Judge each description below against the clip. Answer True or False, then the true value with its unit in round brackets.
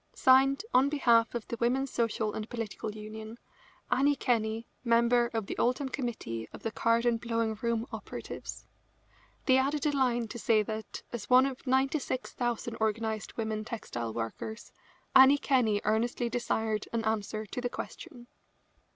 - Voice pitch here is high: True (235 Hz)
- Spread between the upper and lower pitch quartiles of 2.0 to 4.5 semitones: True (2.6 semitones)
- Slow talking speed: False (150 wpm)